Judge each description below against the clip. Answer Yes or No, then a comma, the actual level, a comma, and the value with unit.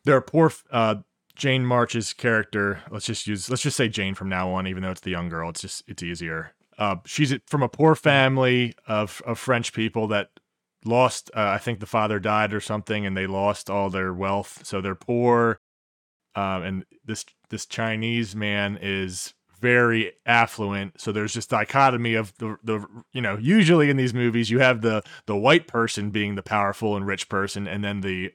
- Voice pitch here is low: Yes, low, 110 Hz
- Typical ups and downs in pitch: Yes, average, 3.6 semitones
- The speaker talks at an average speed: Yes, average, 195 wpm